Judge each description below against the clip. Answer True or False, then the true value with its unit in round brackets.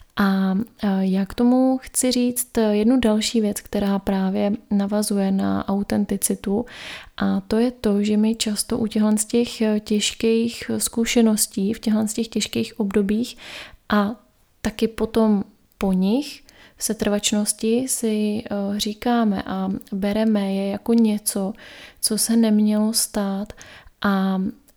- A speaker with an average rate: True (125 wpm)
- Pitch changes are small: True (2.0 semitones)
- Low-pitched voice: False (215 Hz)